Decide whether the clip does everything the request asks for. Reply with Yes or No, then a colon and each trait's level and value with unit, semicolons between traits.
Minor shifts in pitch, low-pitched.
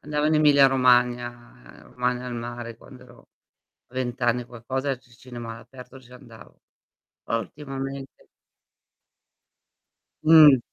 Yes: narrow, 2.1 semitones; low, 125 Hz